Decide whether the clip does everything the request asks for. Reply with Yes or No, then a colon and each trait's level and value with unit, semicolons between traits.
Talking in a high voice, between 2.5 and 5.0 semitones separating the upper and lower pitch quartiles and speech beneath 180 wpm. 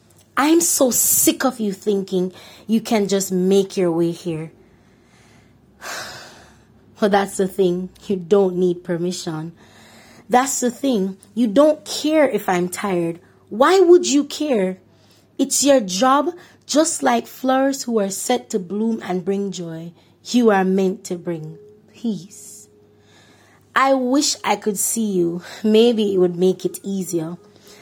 No: high, 200 Hz; wide, 5.5 semitones; average, 140 wpm